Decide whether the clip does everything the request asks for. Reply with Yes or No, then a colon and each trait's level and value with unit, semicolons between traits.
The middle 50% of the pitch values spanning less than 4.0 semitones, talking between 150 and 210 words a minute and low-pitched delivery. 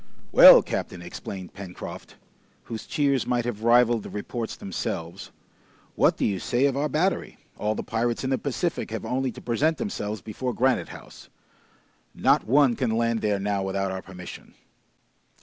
No: average, 4.3 semitones; average, 165 wpm; low, 115 Hz